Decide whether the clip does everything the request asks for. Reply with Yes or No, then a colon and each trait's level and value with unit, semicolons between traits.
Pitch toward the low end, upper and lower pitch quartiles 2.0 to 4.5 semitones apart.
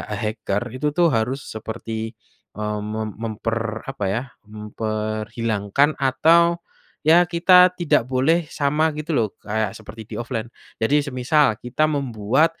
No: low, 115 Hz; wide, 5.5 semitones